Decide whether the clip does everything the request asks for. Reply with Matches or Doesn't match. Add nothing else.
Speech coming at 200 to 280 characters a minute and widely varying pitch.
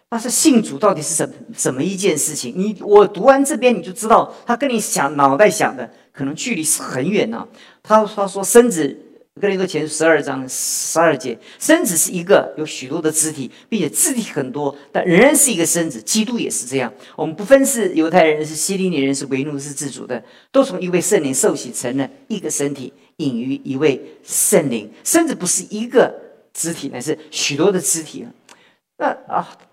Doesn't match